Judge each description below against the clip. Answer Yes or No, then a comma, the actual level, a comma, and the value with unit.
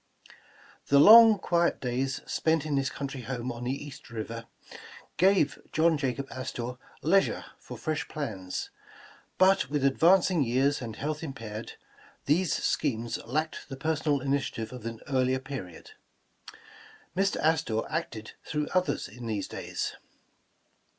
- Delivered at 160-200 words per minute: No, slow, 135 wpm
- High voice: No, medium, 140 Hz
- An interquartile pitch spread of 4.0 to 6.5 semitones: Yes, average, 4.5 semitones